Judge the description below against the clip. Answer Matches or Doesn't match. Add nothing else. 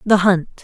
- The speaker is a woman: Matches